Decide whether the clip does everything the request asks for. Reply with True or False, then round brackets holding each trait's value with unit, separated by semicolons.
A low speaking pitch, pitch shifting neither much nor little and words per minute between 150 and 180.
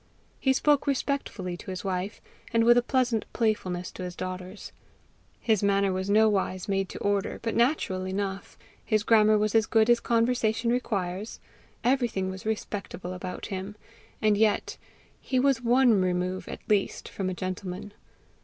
False (205 Hz; 3.7 semitones; 155 wpm)